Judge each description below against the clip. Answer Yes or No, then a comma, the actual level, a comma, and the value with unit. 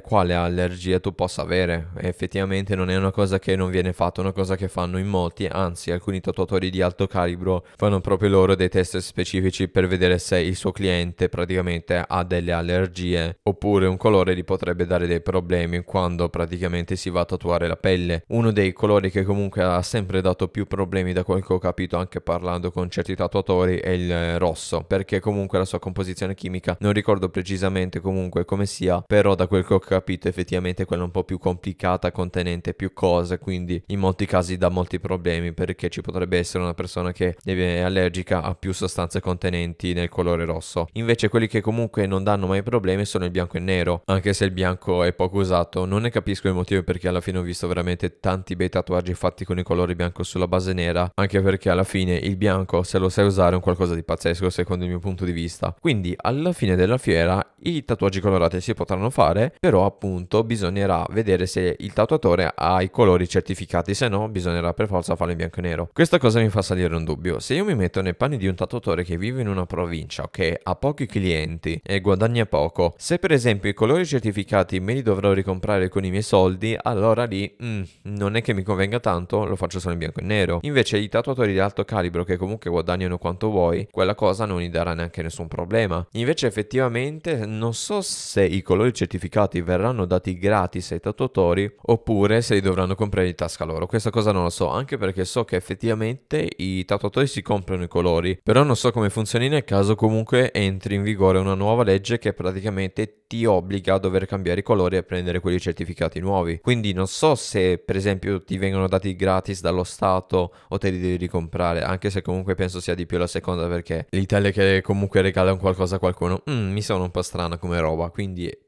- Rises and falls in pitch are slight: Yes, narrow, 2.0 semitones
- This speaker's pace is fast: Yes, fast, 210 wpm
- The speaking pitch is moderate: No, very low, 95 Hz